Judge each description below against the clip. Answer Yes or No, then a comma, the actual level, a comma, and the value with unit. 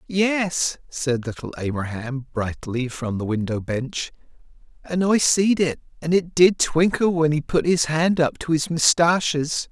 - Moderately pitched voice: Yes, medium, 155 Hz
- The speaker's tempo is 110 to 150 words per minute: No, average, 160 wpm